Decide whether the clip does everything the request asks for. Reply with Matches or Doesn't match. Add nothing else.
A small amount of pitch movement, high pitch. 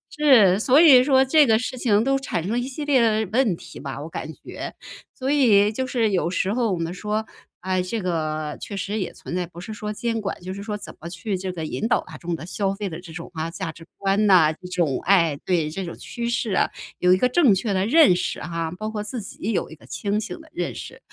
Doesn't match